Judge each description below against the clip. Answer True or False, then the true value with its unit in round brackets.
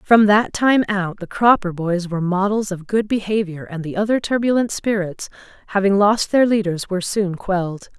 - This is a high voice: True (200 Hz)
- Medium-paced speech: True (180 wpm)